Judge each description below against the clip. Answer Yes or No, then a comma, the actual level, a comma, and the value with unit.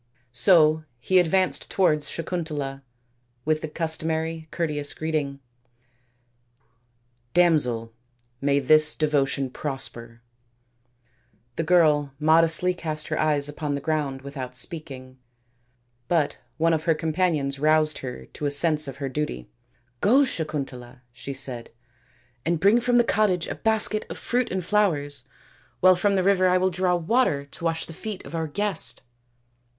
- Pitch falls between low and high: Yes, medium, 155 Hz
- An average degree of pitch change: Yes, average, 4.0 semitones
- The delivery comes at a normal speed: Yes, average, 145 wpm